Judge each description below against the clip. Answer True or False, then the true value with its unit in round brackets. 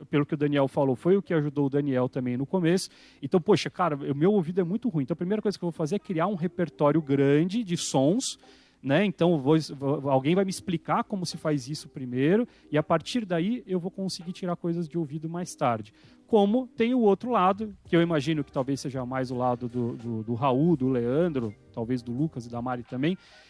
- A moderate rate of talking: False (230 wpm)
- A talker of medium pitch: True (160 Hz)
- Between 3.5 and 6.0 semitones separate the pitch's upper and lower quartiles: True (5.0 semitones)